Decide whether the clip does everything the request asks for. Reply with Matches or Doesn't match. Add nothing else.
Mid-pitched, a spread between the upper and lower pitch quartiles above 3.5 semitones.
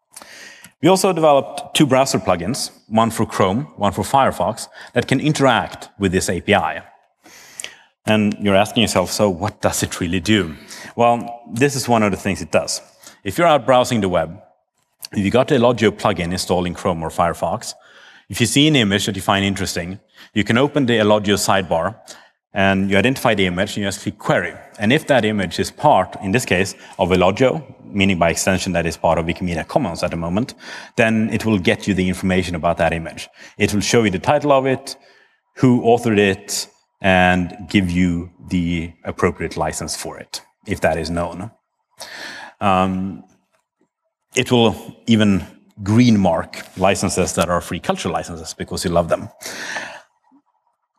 Doesn't match